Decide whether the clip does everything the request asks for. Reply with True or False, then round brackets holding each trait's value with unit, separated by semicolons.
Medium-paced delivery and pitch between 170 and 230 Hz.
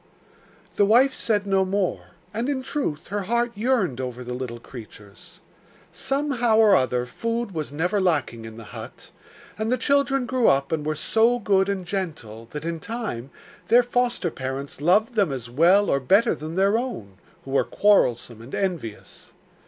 True (170 wpm; 190 Hz)